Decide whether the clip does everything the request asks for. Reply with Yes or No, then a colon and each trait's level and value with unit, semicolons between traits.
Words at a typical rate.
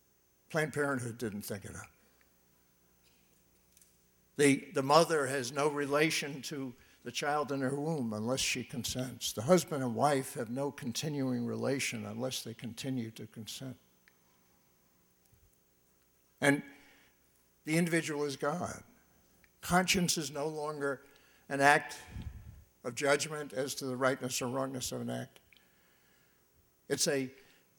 No: slow, 125 wpm